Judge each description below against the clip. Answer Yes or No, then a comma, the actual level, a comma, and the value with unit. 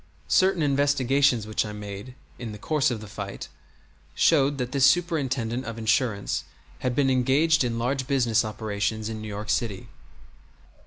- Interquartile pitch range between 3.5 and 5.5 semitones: Yes, average, 4.2 semitones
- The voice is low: Yes, low, 120 Hz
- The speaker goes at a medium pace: Yes, average, 155 wpm